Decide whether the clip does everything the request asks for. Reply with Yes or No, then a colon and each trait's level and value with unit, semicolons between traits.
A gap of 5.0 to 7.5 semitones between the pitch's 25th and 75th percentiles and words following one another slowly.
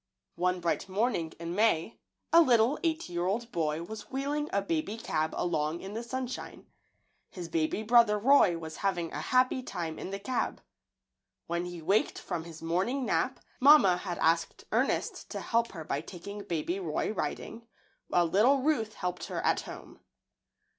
No: wide, 5.6 semitones; average, 165 wpm